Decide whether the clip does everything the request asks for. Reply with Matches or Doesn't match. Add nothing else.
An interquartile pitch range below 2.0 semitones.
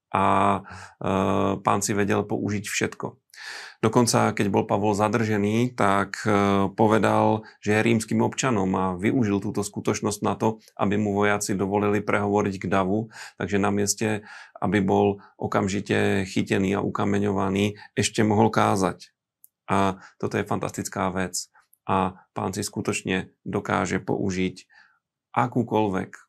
Matches